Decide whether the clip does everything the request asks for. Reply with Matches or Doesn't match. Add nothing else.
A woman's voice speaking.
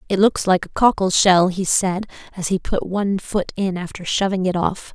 Matches